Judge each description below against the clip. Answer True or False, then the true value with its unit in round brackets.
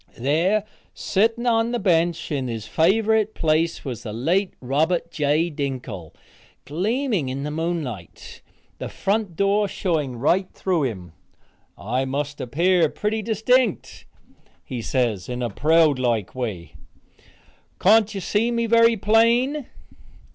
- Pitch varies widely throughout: True (8.4 semitones)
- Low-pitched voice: False (165 Hz)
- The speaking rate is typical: False (130 wpm)